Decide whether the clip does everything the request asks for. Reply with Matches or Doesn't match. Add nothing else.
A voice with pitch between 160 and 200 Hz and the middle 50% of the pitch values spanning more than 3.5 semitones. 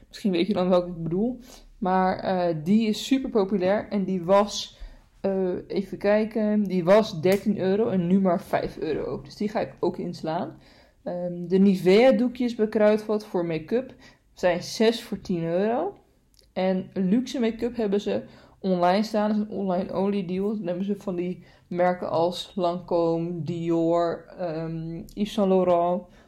Doesn't match